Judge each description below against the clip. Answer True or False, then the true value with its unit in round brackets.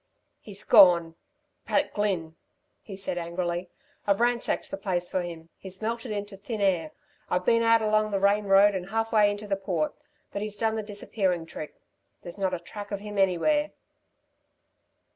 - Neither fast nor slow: True (175 wpm)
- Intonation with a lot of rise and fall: False (3.0 semitones)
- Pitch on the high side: True (200 Hz)